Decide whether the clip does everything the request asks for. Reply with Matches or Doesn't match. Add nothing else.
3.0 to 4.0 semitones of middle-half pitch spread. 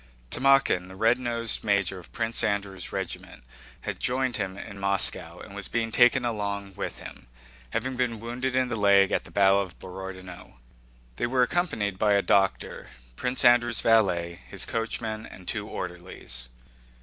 Matches